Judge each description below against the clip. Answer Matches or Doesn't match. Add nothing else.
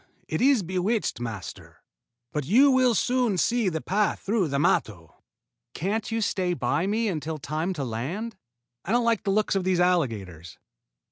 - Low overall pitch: Doesn't match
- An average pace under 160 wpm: Doesn't match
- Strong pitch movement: Matches